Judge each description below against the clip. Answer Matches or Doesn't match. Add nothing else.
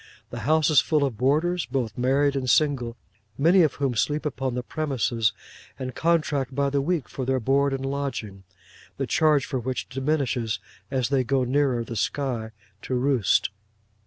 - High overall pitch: Doesn't match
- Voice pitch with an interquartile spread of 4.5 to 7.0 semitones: Doesn't match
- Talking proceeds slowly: Doesn't match